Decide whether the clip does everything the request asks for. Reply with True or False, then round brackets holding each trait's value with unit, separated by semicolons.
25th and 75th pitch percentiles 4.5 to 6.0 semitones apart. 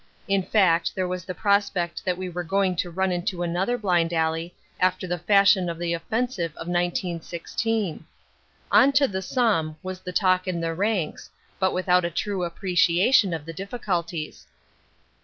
False (2.5 semitones)